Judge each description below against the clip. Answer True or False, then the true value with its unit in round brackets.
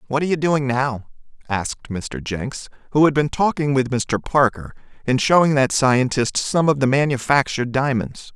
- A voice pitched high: False (135 Hz)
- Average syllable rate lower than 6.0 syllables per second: True (4.9 syllables/s)